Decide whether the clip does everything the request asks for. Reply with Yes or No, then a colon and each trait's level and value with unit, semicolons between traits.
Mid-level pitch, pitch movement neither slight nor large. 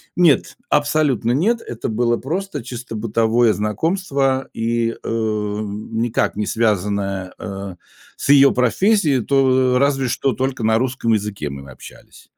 No: low, 120 Hz; average, 4.2 semitones